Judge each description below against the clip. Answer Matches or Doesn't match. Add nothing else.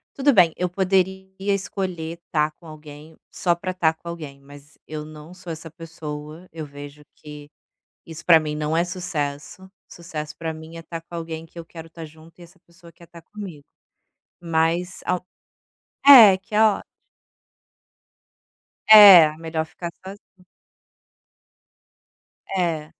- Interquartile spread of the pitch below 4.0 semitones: Matches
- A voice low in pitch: Doesn't match